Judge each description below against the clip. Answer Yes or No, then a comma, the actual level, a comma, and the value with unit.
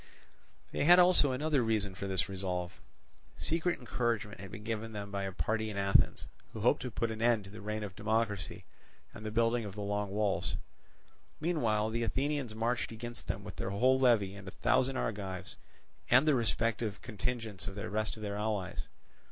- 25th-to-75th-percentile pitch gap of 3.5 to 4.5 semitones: No, average, 2.9 semitones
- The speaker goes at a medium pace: Yes, average, 190 wpm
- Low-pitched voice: Yes, low, 110 Hz